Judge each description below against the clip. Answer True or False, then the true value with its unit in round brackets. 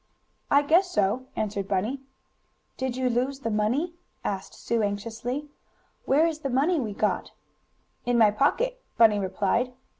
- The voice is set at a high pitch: True (245 Hz)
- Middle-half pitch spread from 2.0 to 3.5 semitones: False (5.0 semitones)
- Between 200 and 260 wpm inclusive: False (145 wpm)